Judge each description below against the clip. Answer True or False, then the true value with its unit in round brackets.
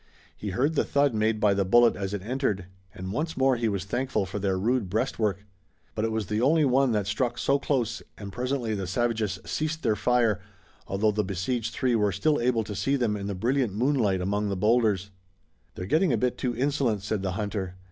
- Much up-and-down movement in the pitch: False (4.1 semitones)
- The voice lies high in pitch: False (110 Hz)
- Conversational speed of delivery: False (215 wpm)